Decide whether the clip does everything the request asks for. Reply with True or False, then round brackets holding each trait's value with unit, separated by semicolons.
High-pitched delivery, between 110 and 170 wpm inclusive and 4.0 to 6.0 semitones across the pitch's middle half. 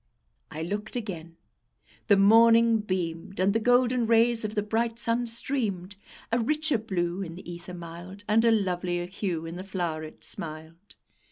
True (200 Hz; 160 wpm; 4.6 semitones)